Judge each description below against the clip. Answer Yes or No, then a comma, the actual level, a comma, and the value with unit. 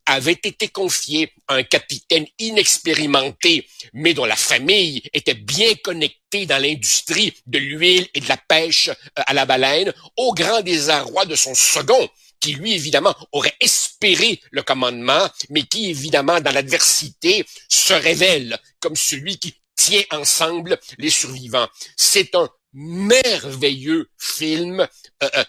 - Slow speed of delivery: Yes, slow, 135 wpm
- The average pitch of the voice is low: No, medium, 160 Hz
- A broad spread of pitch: Yes, wide, 5.8 semitones